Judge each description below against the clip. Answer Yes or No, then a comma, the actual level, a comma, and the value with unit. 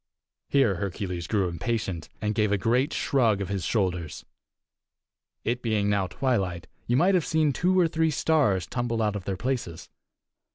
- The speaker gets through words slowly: No, average, 165 wpm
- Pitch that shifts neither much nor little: No, wide, 5.7 semitones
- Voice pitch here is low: Yes, low, 110 Hz